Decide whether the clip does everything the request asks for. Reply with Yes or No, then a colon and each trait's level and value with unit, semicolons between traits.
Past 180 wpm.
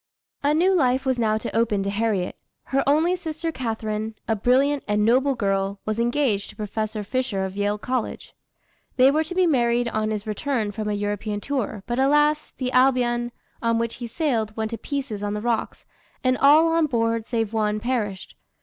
Yes: average, 190 wpm